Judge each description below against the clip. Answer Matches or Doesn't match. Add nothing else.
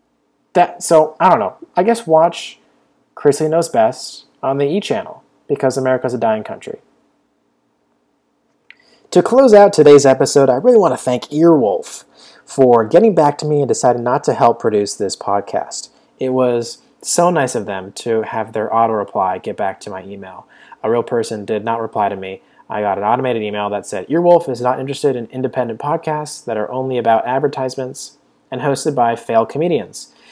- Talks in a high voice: Doesn't match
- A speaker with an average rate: Matches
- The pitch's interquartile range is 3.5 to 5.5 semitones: Matches